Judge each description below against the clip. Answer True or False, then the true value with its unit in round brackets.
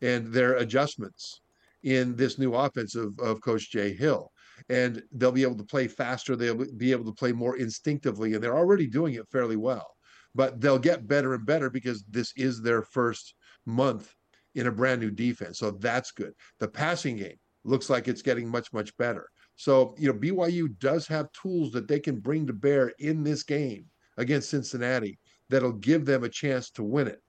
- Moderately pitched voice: False (130 Hz)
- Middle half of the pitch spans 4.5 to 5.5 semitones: False (3.2 semitones)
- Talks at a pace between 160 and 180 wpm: False (195 wpm)